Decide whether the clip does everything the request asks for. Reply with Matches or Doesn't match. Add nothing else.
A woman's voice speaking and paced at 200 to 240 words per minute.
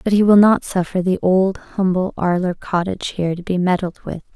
Matches